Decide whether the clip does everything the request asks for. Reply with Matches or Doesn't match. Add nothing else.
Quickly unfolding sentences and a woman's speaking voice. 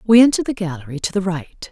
Matches